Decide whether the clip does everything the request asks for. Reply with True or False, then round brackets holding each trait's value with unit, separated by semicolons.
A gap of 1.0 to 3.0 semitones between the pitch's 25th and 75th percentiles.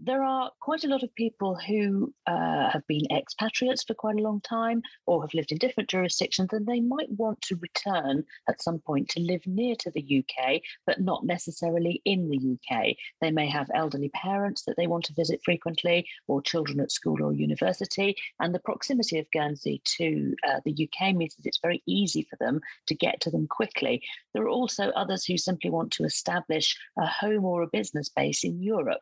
False (5.5 semitones)